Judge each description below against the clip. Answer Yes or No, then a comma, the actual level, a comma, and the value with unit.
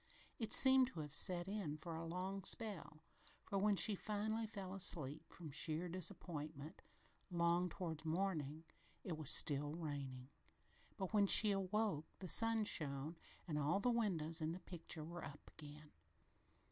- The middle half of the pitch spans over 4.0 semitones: Yes, average, 4.4 semitones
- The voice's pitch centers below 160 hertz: No, medium, 170 Hz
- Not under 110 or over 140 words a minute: No, average, 155 wpm